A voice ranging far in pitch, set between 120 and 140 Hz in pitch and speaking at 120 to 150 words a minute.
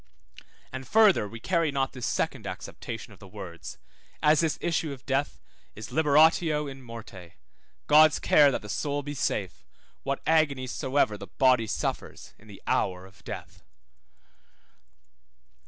Yes: wide, 6.1 semitones; low, 135 Hz; average, 145 wpm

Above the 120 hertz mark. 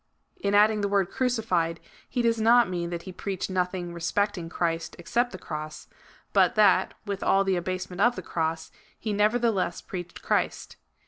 Yes: high, 190 Hz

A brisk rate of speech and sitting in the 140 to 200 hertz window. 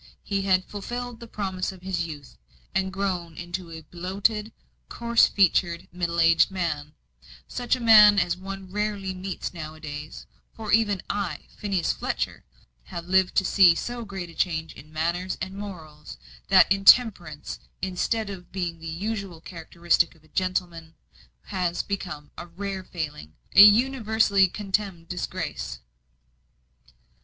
No: average, 145 wpm; medium, 185 Hz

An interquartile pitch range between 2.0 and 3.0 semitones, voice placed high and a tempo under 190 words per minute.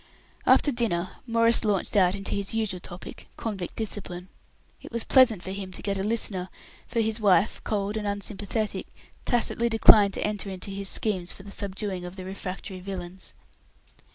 Yes: average, 2.7 semitones; high, 200 Hz; average, 170 wpm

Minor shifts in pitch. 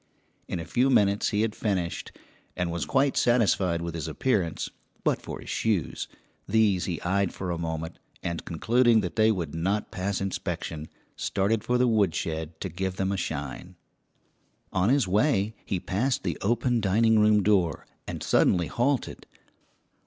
No: average, 4.4 semitones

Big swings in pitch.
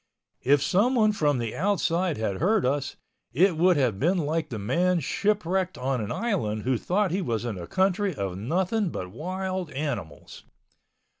Yes: wide, 7.5 semitones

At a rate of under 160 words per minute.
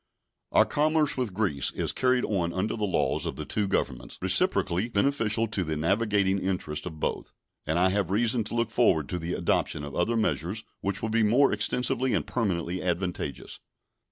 No: average, 185 wpm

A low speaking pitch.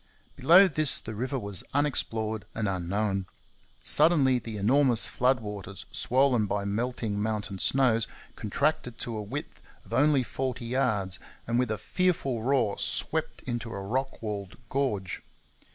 Yes: low, 115 Hz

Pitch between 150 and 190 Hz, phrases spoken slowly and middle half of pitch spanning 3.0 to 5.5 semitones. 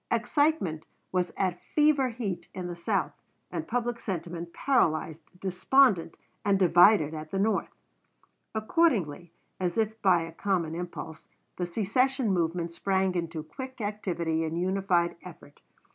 Yes: medium, 185 Hz; slow, 130 wpm; average, 4.5 semitones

